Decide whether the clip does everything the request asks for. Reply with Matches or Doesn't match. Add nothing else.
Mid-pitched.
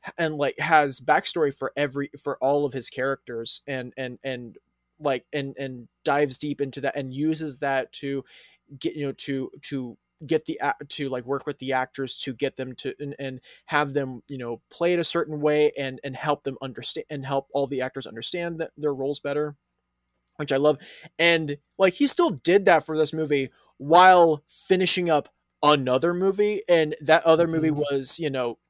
Matches